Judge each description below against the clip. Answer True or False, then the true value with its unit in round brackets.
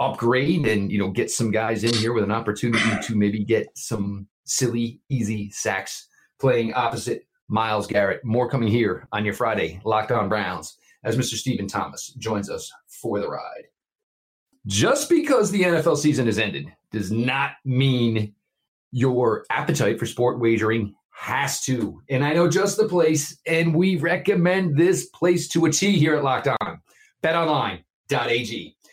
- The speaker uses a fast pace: False (160 wpm)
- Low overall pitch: True (125 Hz)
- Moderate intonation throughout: False (6.8 semitones)